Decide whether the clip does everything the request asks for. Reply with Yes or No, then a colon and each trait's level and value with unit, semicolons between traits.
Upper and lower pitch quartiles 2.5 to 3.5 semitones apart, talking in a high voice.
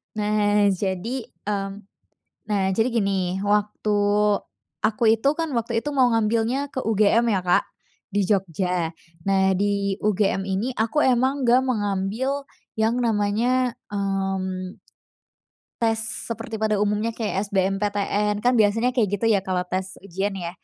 Yes: average, 2.8 semitones; high, 210 Hz